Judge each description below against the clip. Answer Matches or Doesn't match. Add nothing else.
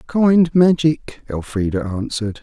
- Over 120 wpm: Doesn't match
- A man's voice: Matches